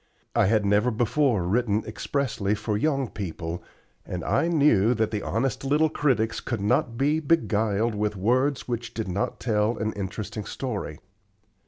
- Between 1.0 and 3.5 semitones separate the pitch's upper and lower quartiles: No, average, 4.2 semitones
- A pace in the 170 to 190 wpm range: No, average, 155 wpm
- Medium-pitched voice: No, low, 110 Hz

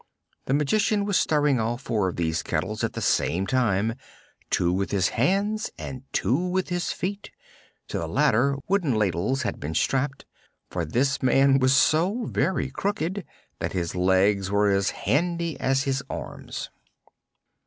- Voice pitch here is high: No, low, 135 Hz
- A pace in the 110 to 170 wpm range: Yes, average, 155 wpm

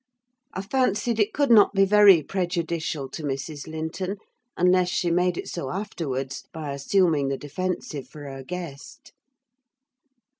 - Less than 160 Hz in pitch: No, medium, 170 Hz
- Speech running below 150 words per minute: Yes, average, 140 wpm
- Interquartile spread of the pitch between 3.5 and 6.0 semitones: Yes, average, 5.0 semitones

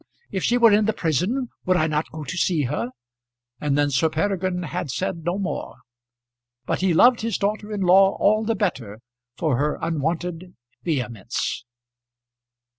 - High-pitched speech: No, medium, 175 Hz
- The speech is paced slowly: No, average, 165 wpm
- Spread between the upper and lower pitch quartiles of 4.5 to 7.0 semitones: Yes, average, 4.9 semitones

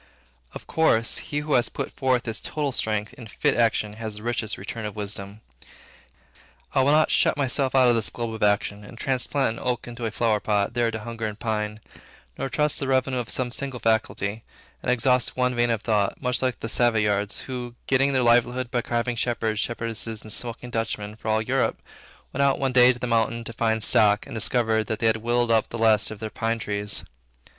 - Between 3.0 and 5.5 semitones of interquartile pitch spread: No, narrow, 2.4 semitones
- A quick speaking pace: Yes, fast, 215 wpm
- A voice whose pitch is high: No, low, 115 Hz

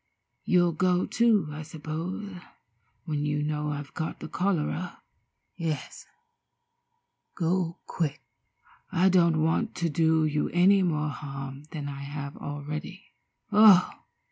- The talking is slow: Yes, slow, 120 wpm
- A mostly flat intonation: No, average, 3.4 semitones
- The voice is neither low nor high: Yes, medium, 160 Hz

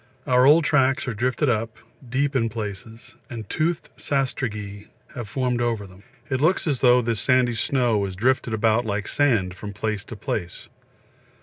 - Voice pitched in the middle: No, low, 120 Hz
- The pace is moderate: Yes, average, 170 wpm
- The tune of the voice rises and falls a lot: No, average, 3.7 semitones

